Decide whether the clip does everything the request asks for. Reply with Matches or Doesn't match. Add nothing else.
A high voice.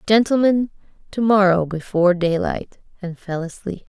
Matches